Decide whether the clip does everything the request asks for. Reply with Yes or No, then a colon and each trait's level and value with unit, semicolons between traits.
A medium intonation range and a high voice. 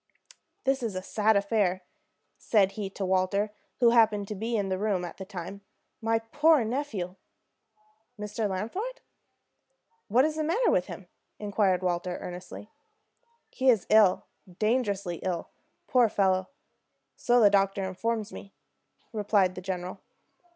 Yes: average, 3.3 semitones; high, 205 Hz